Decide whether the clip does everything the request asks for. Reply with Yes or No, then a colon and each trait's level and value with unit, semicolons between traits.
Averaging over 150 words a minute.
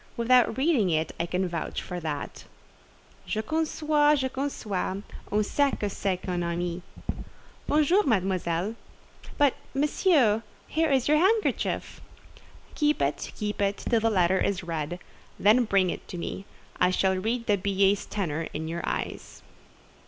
No: average, 145 wpm